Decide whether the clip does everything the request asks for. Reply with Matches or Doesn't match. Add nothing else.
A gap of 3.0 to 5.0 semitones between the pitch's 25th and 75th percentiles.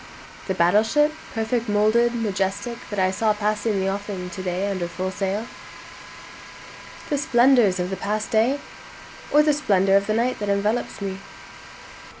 Matches